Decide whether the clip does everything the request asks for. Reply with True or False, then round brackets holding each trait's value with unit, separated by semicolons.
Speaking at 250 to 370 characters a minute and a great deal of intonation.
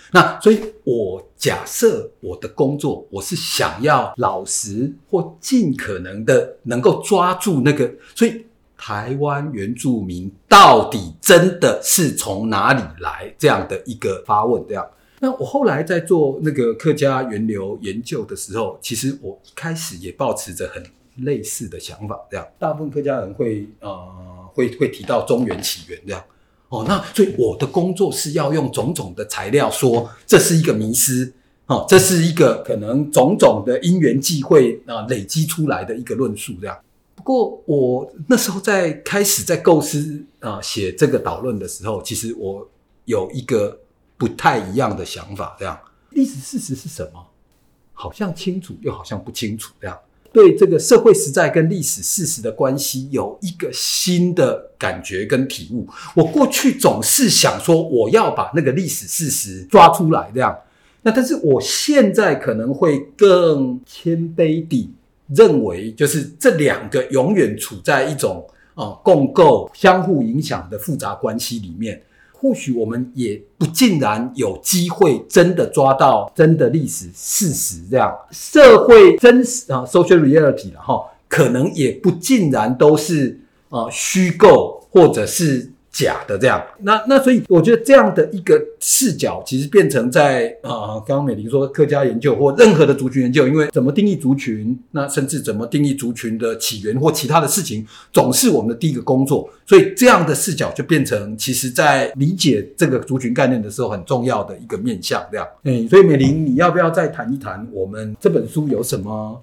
True (270 characters per minute; 7.5 semitones)